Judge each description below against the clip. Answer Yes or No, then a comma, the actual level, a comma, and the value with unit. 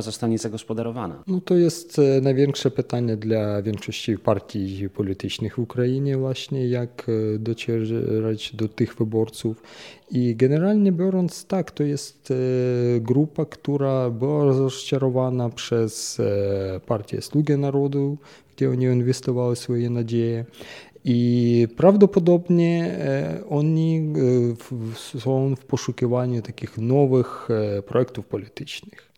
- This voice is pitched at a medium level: No, low, 125 Hz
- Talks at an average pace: No, slow, 95 wpm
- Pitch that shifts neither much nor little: Yes, average, 3.6 semitones